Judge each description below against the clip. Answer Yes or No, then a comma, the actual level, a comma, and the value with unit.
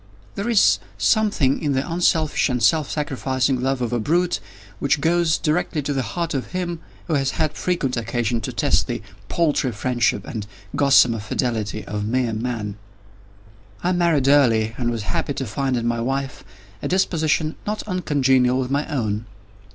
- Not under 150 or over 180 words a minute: Yes, average, 165 wpm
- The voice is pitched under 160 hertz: Yes, low, 135 Hz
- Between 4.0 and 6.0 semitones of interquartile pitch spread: Yes, average, 5.0 semitones